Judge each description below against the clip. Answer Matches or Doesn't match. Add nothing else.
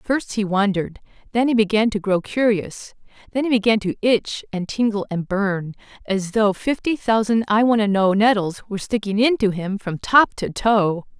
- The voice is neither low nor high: Doesn't match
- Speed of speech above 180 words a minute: Matches